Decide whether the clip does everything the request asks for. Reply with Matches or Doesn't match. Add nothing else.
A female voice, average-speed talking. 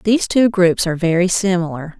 Matches